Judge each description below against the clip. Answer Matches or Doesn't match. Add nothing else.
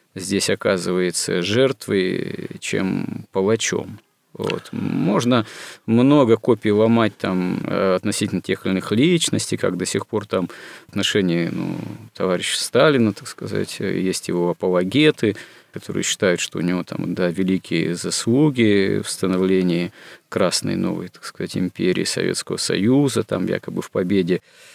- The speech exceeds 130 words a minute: Doesn't match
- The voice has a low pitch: Matches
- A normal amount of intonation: Matches